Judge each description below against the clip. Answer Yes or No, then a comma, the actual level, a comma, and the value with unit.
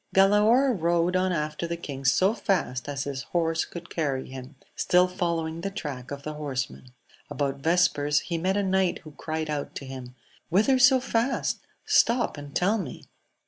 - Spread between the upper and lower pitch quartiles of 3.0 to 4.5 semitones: No, average, 4.9 semitones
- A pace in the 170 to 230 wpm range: Yes, average, 175 wpm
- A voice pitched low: No, medium, 165 Hz